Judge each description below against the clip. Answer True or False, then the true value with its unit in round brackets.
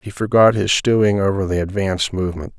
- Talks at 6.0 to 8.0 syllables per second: True (6.1 syllables/s)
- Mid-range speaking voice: False (100 Hz)